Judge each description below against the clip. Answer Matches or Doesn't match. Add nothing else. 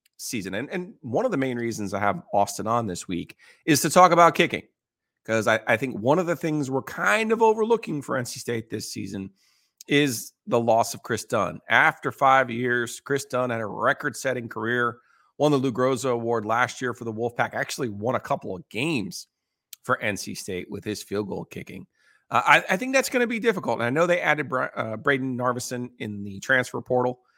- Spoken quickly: Matches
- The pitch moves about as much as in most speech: Matches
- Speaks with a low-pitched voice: Matches